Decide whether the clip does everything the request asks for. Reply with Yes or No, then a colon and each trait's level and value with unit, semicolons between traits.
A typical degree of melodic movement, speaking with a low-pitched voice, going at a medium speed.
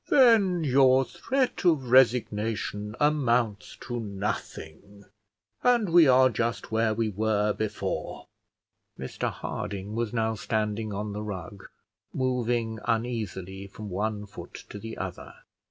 No: average, 3.7 semitones; low, 110 Hz; slow, 120 wpm